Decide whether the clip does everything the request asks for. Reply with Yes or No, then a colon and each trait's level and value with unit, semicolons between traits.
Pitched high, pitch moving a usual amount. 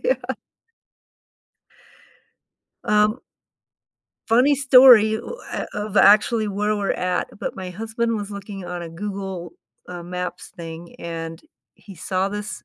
Yes: high, 200 Hz; average, 3.3 semitones